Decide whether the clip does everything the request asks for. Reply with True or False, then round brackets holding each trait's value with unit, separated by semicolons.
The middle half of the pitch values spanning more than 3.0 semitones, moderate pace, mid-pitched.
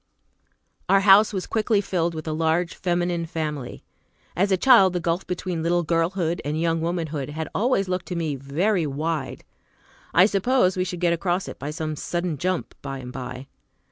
False (2.7 semitones; 180 wpm; 170 Hz)